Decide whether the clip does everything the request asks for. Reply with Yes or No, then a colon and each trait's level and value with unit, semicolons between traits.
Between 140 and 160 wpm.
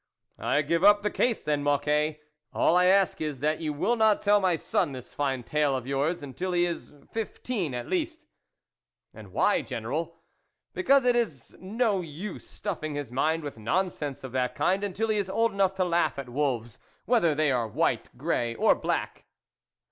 No: average, 195 wpm